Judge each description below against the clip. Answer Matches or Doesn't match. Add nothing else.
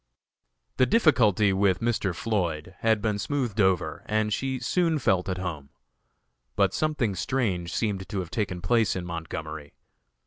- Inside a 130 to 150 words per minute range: Matches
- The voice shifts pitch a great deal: Doesn't match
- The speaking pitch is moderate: Doesn't match